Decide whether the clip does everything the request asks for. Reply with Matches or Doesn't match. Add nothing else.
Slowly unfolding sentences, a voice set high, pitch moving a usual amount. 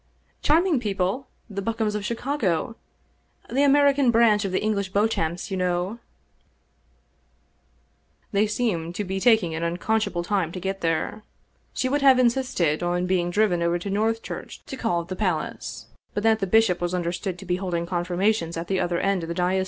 Doesn't match